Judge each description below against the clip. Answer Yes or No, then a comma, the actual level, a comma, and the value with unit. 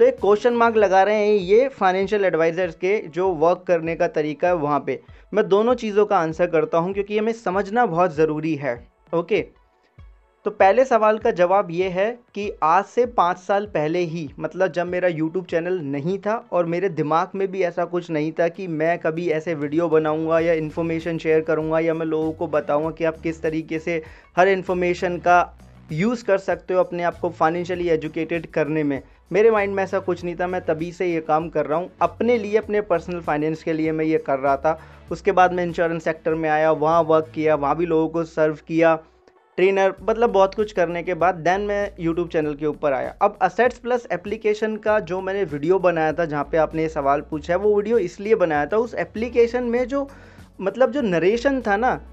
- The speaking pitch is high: No, medium, 175 Hz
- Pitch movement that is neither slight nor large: Yes, average, 3.8 semitones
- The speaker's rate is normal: No, fast, 215 wpm